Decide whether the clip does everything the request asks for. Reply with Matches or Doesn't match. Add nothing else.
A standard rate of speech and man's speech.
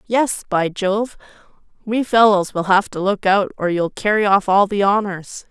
Doesn't match